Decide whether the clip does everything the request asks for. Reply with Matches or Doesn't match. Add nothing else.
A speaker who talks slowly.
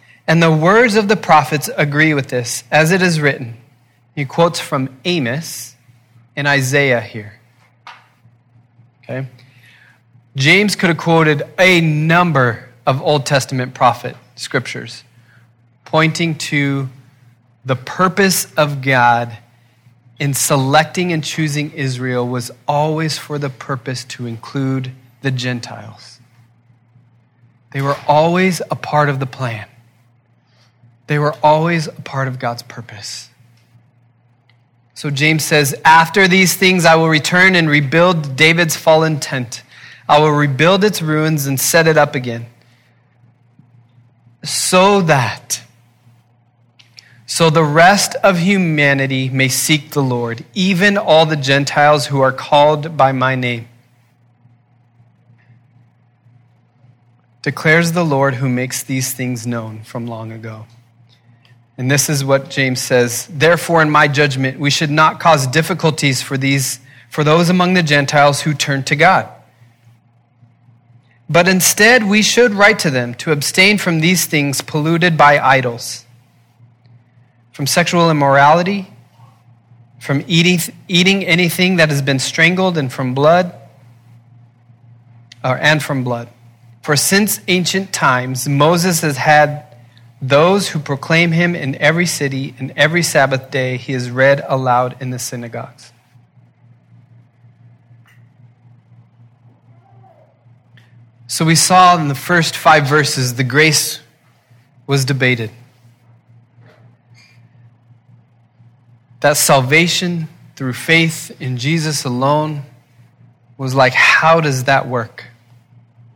Matches